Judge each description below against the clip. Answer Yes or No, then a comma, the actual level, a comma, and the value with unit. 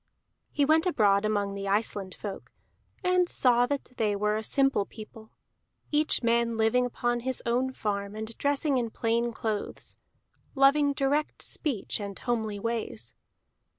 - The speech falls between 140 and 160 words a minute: Yes, average, 145 wpm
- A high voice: Yes, high, 230 Hz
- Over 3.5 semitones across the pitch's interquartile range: Yes, average, 4.4 semitones